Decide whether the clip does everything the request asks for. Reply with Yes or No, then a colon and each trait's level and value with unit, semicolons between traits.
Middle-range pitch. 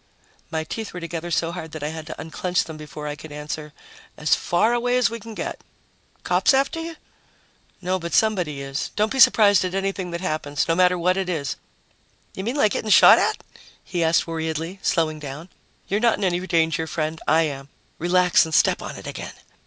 Yes: medium, 170 Hz